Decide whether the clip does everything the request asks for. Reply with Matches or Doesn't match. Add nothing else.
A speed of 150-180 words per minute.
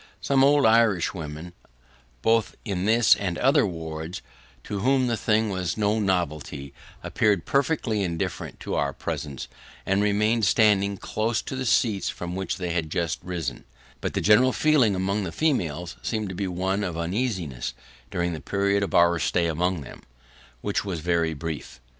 Matches